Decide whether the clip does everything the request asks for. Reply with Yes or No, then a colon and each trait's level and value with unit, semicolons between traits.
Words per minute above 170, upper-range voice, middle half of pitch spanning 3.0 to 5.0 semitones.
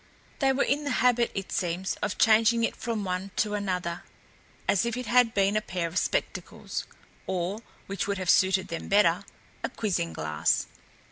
Yes: average, 180 wpm; high, 200 Hz; average, 3.9 semitones